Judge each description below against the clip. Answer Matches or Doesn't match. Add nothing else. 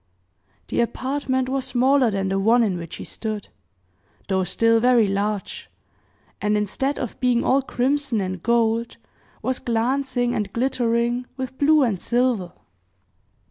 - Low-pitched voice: Doesn't match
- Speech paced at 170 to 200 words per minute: Doesn't match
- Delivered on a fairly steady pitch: Doesn't match